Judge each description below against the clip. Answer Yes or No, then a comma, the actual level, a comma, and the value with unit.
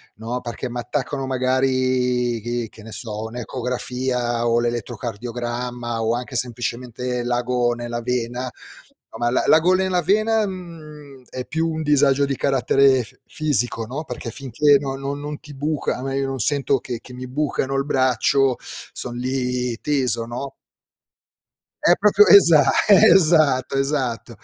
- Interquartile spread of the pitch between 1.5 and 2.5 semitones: No, average, 2.9 semitones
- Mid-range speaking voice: No, low, 130 Hz